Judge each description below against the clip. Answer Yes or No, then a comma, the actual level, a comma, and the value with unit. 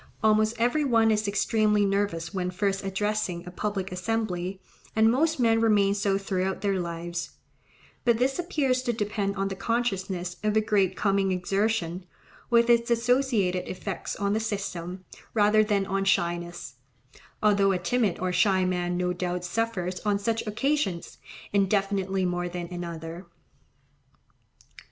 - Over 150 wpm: No, average, 145 wpm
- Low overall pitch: No, high, 195 Hz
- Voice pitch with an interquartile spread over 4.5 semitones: No, average, 3.4 semitones